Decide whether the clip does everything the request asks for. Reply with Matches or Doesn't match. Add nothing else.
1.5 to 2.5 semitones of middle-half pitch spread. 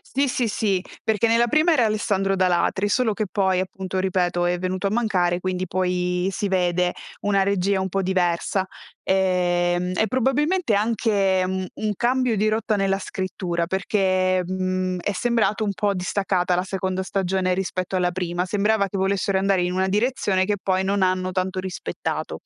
Matches